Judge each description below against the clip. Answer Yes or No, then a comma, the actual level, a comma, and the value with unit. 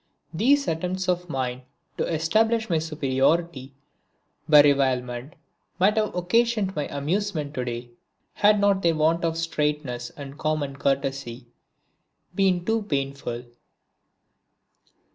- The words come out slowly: Yes, slow, 115 wpm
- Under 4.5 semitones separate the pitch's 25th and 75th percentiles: No, average, 5.3 semitones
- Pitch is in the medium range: Yes, medium, 155 Hz